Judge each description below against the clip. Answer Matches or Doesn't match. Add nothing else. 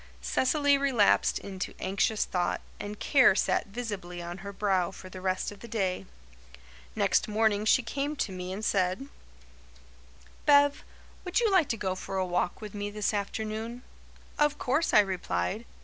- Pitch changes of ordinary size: Matches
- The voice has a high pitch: Matches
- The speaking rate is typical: Matches